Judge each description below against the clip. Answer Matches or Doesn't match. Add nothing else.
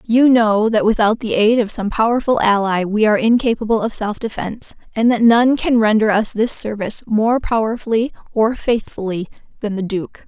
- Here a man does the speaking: Doesn't match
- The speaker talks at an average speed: Matches